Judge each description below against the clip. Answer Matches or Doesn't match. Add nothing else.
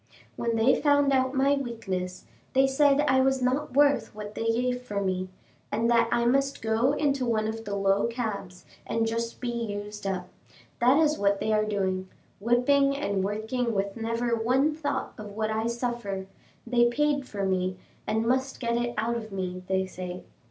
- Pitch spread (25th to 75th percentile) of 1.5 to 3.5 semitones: Doesn't match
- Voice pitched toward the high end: Matches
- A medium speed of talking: Matches